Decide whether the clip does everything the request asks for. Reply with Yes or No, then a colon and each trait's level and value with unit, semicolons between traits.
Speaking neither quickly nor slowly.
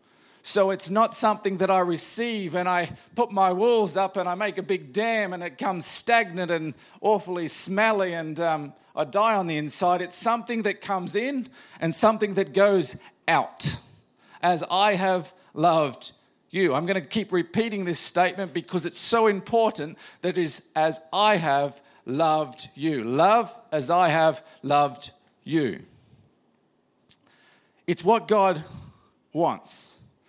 Yes: average, 155 wpm